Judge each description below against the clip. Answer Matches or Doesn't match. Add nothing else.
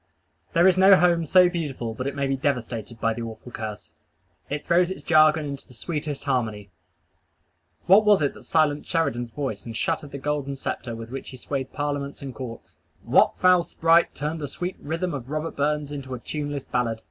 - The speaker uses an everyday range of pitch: Matches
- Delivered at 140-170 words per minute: Doesn't match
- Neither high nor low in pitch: Matches